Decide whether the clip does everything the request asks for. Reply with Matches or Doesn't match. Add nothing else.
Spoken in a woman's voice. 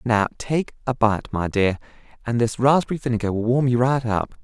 Doesn't match